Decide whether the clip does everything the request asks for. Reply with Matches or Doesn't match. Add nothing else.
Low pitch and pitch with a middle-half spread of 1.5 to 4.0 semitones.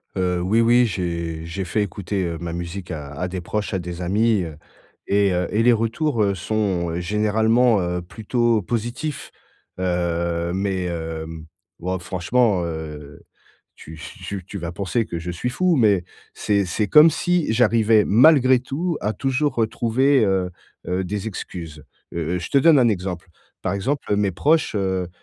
Doesn't match